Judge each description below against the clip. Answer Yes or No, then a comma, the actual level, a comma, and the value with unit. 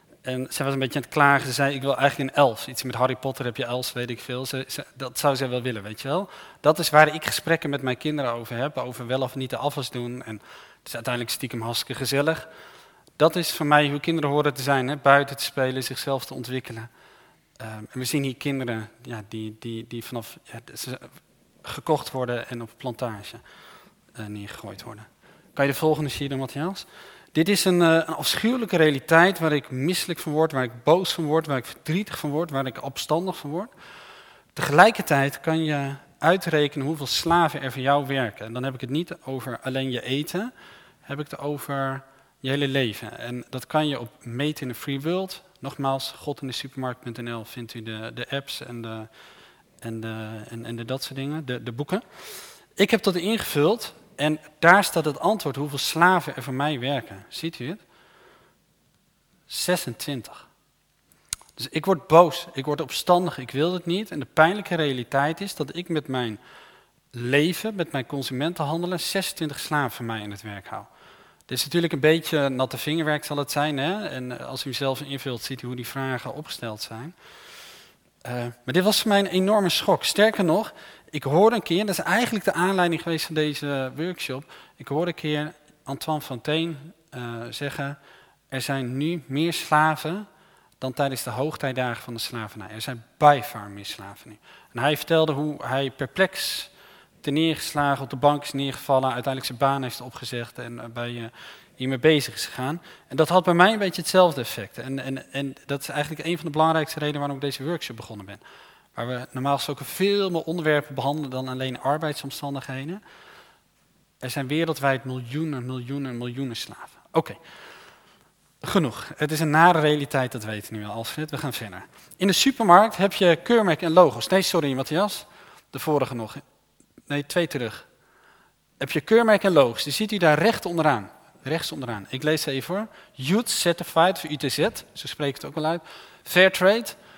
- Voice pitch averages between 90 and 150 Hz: Yes, medium, 140 Hz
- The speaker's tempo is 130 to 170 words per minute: No, average, 195 wpm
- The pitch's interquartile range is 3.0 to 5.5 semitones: Yes, average, 4.0 semitones